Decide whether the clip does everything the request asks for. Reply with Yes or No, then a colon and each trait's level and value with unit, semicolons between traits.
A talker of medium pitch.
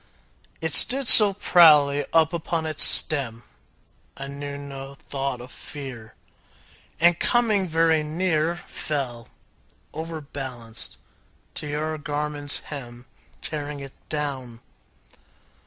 Yes: medium, 145 Hz